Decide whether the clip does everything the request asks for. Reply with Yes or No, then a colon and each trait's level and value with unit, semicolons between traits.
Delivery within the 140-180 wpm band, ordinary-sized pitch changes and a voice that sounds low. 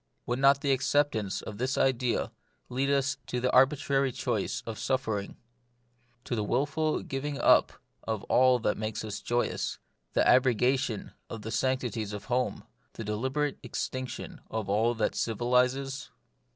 Yes: average, 150 wpm; average, 3.3 semitones; low, 125 Hz